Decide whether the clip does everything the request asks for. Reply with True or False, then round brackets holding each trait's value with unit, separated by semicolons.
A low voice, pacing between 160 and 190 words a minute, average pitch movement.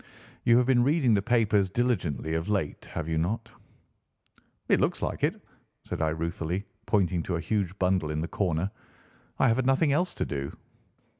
False (95 Hz; 180 wpm; 6.4 semitones)